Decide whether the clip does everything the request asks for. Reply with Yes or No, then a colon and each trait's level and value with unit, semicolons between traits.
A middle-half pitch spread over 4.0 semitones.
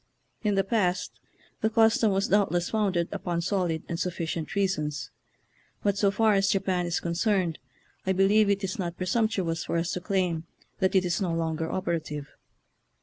No: average, 3.0 semitones